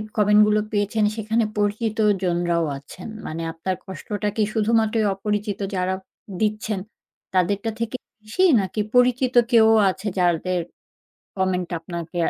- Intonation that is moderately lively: Yes, average, 3.1 semitones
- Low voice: No, high, 205 Hz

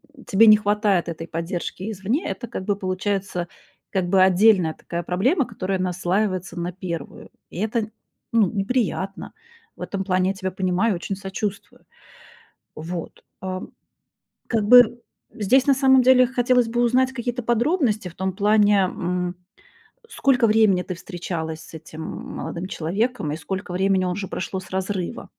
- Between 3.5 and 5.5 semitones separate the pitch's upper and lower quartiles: Yes, average, 3.9 semitones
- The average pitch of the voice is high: Yes, high, 195 Hz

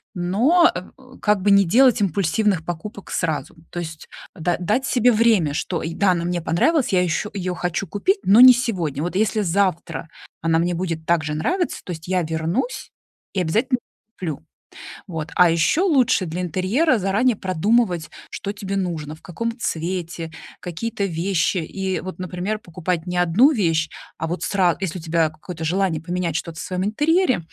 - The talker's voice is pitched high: No, medium, 180 Hz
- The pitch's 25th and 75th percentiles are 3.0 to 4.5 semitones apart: Yes, average, 4.2 semitones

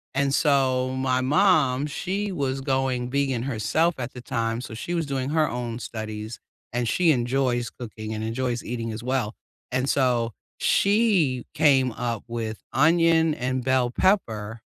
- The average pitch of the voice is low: Yes, low, 130 Hz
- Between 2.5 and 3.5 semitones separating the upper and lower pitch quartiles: Yes, average, 3.1 semitones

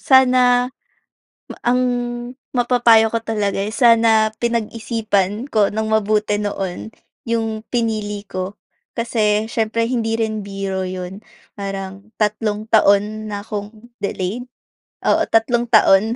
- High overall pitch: Yes, high, 220 Hz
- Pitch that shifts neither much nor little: No, narrow, 2.1 semitones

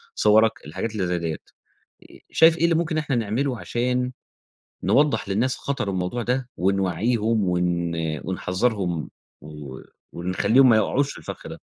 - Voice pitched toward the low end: Yes, low, 110 Hz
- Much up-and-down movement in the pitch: Yes, wide, 5.8 semitones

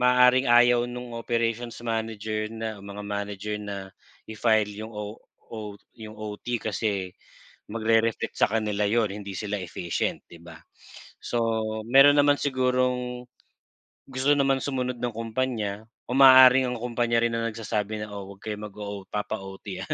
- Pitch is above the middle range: No, low, 115 Hz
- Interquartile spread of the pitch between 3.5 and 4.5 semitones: No, average, 3.0 semitones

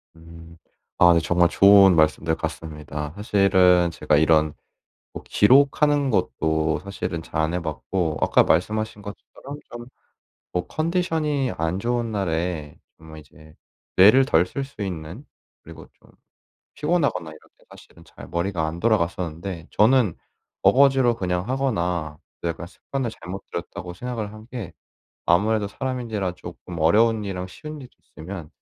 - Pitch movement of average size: No, wide, 6.0 semitones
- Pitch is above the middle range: No, very low, 95 Hz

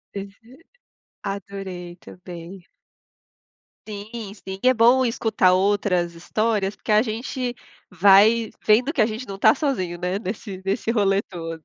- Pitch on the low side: No, high, 200 Hz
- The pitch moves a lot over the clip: No, average, 3.4 semitones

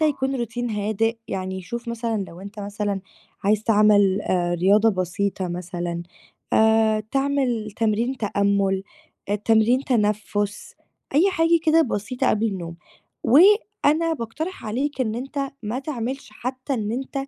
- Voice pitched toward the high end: Yes, high, 220 Hz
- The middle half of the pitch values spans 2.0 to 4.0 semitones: No, average, 4.5 semitones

